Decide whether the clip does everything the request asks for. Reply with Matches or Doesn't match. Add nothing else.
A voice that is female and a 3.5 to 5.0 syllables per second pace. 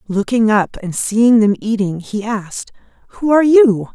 Matches